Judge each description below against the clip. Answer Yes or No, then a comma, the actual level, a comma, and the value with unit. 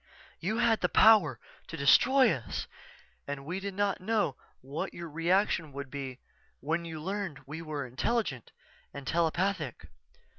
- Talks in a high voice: No, medium, 165 Hz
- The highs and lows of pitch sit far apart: Yes, wide, 6.0 semitones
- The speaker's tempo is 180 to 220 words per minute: No, average, 145 wpm